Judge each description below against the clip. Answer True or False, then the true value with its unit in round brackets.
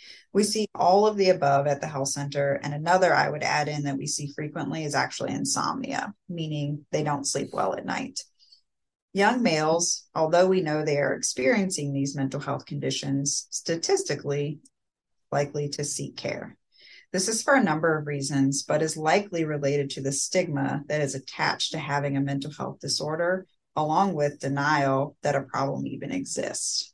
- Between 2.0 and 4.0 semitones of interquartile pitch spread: True (3.6 semitones)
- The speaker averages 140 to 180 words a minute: True (175 wpm)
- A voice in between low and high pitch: True (150 Hz)